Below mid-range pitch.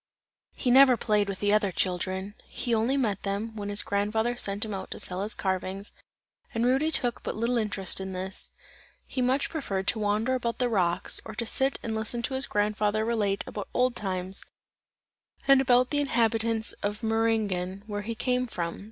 No: high, 220 Hz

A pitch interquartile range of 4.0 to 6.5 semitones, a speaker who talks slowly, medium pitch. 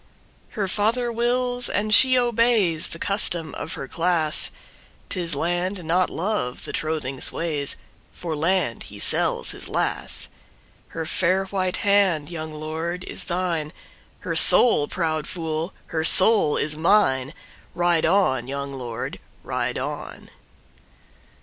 Yes: average, 4.3 semitones; slow, 110 wpm; medium, 170 Hz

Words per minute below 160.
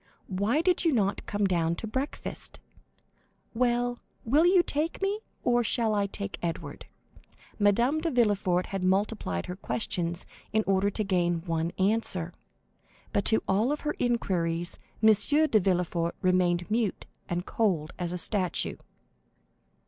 Yes: average, 140 wpm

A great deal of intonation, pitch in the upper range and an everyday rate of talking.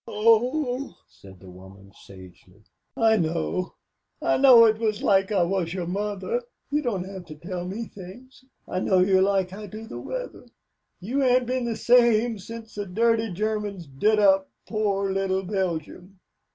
No: average, 4.0 semitones; high, 200 Hz; average, 160 wpm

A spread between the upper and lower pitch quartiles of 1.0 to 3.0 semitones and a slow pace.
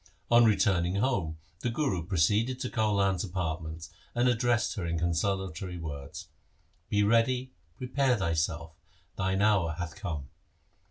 No: wide, 5.6 semitones; slow, 120 wpm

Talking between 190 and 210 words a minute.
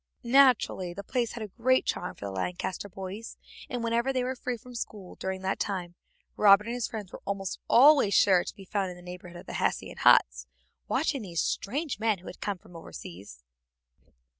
Yes: average, 195 wpm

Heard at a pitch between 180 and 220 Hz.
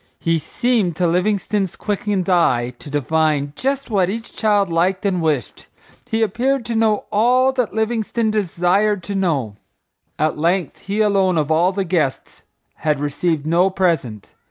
Yes: medium, 185 Hz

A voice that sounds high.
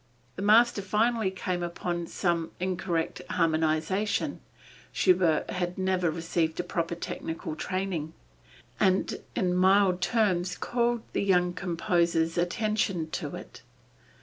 No: medium, 180 Hz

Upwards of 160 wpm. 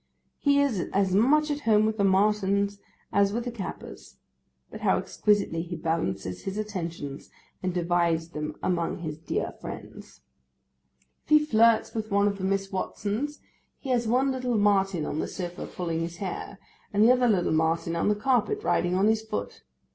Yes: average, 175 wpm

